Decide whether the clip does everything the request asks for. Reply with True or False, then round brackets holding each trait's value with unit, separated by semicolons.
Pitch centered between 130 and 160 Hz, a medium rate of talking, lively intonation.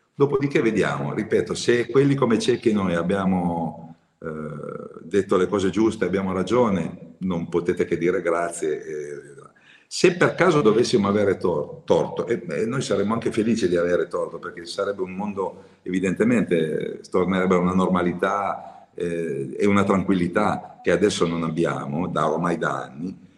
False (95 Hz; 155 wpm; 7.9 semitones)